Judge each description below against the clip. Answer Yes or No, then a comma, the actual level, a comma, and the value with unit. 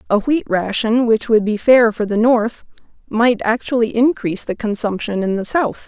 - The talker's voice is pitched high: Yes, high, 225 Hz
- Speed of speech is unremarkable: Yes, average, 185 wpm